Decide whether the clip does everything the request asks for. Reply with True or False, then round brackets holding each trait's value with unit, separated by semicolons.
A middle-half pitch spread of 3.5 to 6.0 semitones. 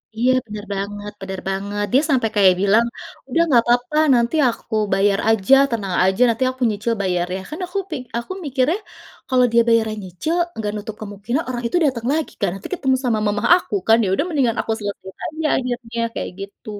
True (4.0 semitones)